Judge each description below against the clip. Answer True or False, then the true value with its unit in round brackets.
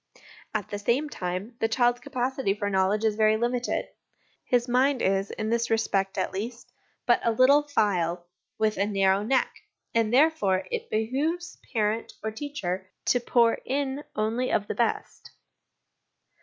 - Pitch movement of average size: True (3.7 semitones)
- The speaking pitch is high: True (225 Hz)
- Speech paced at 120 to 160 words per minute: True (155 wpm)